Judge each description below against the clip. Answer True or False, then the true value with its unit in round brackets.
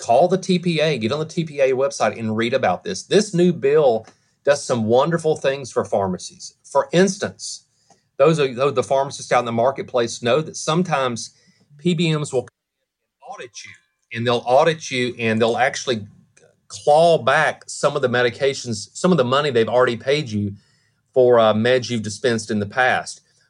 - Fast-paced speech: False (170 wpm)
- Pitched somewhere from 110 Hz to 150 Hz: True (135 Hz)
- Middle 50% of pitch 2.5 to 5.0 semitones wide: False (5.4 semitones)